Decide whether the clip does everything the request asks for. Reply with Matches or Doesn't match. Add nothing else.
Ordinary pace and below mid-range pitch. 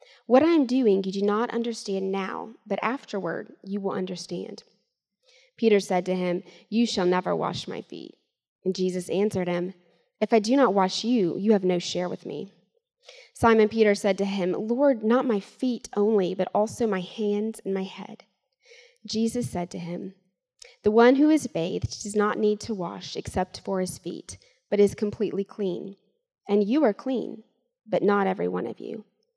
Doesn't match